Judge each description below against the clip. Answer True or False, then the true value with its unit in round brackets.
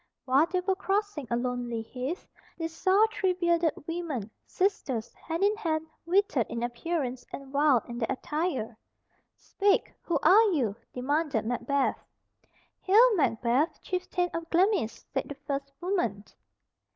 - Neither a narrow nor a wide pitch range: False (6.6 semitones)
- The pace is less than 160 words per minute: True (140 wpm)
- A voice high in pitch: True (315 Hz)